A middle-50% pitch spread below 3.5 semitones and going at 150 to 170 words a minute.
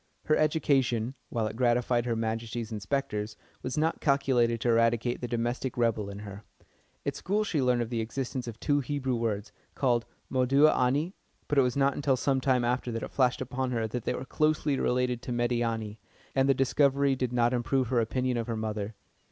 No: narrow, 2.6 semitones; average, 195 wpm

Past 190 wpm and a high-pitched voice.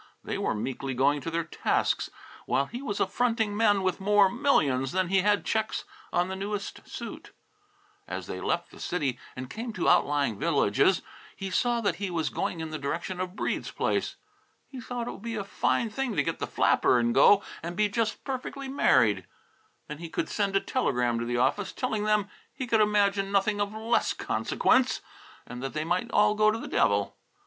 Yes: average, 200 wpm; high, 195 Hz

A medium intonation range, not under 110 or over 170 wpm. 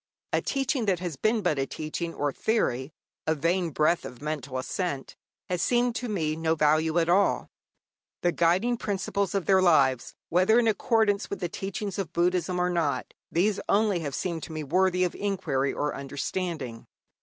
No: average, 4.4 semitones; average, 180 wpm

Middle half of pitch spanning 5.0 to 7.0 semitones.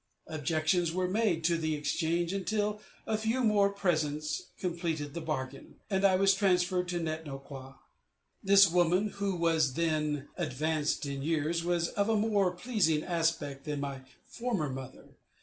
No: average, 4.3 semitones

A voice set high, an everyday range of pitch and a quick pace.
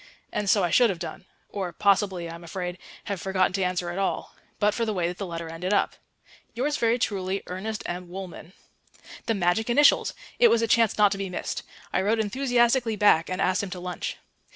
Yes: high, 195 Hz; average, 3.5 semitones; fast, 215 wpm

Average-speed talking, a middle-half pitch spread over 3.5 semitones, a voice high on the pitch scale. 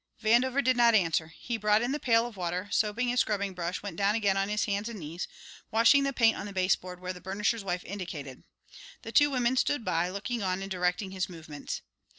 No: fast, 225 wpm; average, 4.3 semitones; high, 200 Hz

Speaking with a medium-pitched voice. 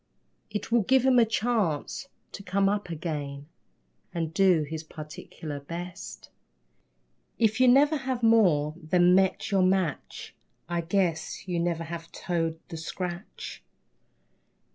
Yes: medium, 180 Hz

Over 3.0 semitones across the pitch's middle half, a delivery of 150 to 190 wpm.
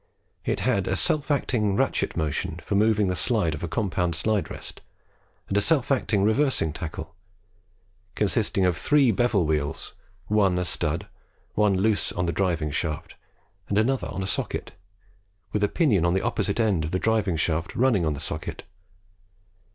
Yes: average, 4.5 semitones; average, 170 wpm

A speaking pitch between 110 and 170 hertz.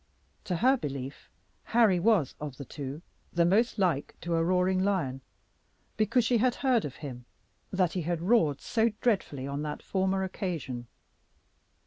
No: medium, 180 Hz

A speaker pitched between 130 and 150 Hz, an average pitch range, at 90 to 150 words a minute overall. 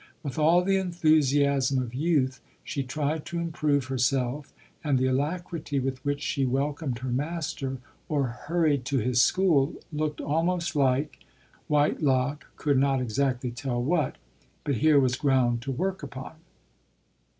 Yes: medium, 140 Hz; average, 3.0 semitones; average, 145 wpm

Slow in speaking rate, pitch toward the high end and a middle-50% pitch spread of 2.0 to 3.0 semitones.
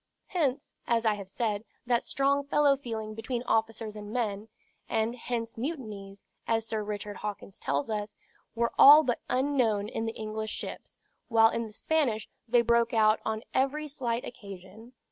No: average, 165 wpm; high, 225 Hz; average, 2.7 semitones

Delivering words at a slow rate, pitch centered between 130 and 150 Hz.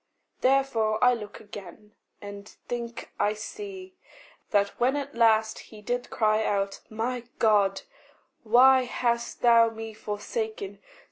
No: slow, 125 wpm; high, 225 Hz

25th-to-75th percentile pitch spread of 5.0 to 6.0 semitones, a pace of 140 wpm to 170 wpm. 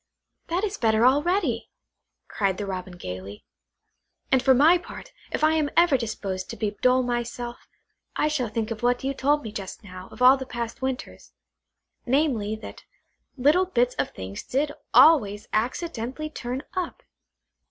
Yes: wide, 5.4 semitones; average, 160 wpm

